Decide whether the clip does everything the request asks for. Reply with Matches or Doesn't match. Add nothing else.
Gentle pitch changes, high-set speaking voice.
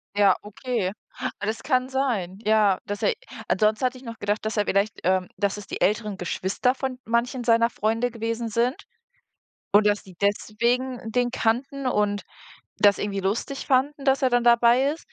Doesn't match